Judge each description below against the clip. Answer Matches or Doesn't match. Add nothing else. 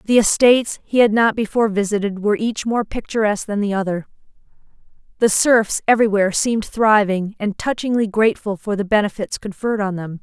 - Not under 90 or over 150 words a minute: Doesn't match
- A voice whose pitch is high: Matches